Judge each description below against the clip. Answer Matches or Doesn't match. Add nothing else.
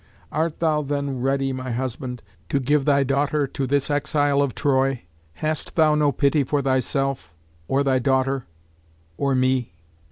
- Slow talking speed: Doesn't match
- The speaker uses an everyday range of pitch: Doesn't match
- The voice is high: Doesn't match